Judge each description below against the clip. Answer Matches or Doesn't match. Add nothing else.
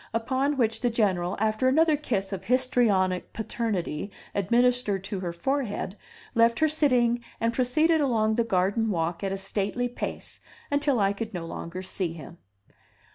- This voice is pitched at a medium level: Doesn't match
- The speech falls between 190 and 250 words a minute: Doesn't match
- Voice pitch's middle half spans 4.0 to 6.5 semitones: Matches